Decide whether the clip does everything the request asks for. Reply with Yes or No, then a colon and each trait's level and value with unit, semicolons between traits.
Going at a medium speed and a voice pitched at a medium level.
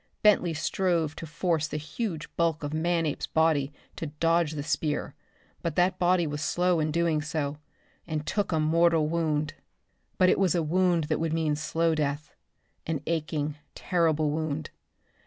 Yes: average, 160 wpm; medium, 160 Hz